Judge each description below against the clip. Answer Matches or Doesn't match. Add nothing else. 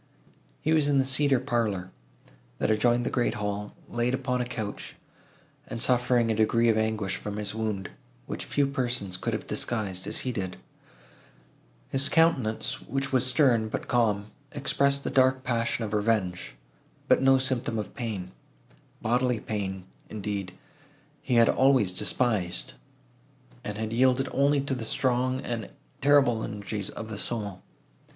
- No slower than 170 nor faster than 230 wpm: Doesn't match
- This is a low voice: Matches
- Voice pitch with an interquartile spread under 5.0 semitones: Matches